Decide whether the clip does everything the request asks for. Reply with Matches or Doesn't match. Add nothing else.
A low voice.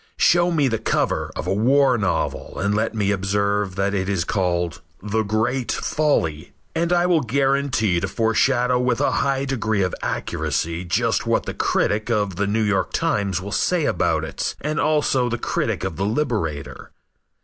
Matches